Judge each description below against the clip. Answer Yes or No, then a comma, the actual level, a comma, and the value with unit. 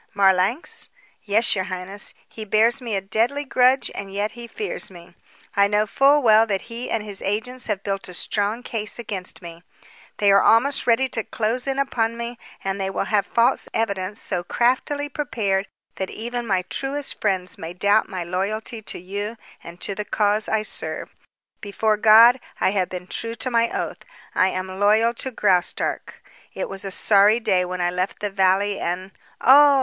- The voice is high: Yes, high, 210 Hz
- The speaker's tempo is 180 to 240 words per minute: Yes, average, 185 wpm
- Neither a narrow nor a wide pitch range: Yes, average, 3.5 semitones